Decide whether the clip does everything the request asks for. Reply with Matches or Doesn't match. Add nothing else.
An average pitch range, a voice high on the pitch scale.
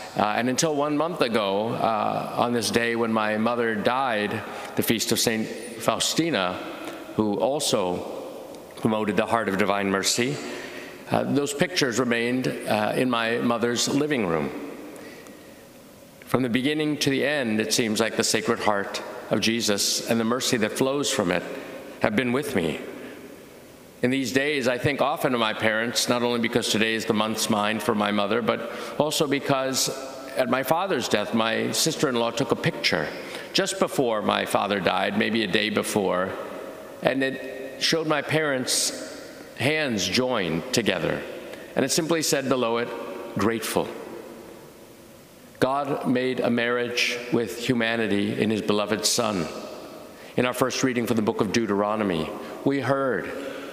Doesn't match